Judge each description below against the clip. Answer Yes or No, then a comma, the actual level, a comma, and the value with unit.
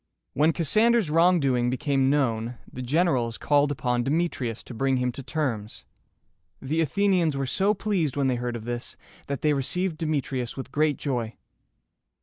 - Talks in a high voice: No, medium, 140 Hz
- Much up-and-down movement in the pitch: No, average, 4.7 semitones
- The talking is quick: No, average, 155 wpm